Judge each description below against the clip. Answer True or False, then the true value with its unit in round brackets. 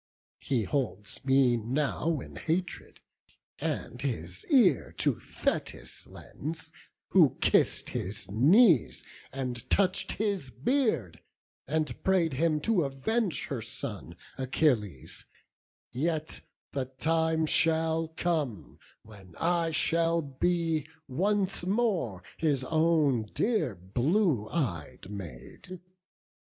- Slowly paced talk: True (100 wpm)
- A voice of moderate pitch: True (155 Hz)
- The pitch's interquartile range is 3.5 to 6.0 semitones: True (5.5 semitones)